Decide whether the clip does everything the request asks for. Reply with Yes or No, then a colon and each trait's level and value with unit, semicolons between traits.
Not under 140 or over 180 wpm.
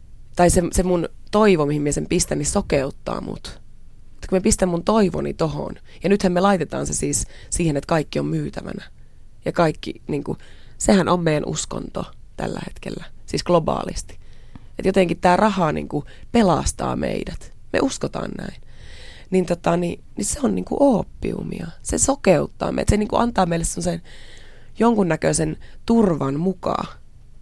Yes: average, 150 wpm